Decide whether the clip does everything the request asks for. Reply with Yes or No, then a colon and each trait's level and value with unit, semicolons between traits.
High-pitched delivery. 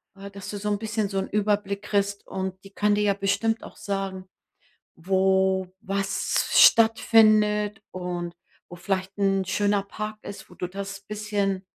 Yes: high, 200 Hz